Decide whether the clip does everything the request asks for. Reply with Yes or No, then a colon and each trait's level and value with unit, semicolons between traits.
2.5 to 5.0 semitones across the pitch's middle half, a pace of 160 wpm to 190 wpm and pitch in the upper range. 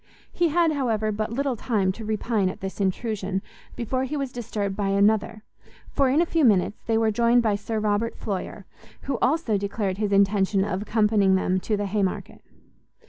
Yes: average, 3.1 semitones; average, 185 wpm; high, 215 Hz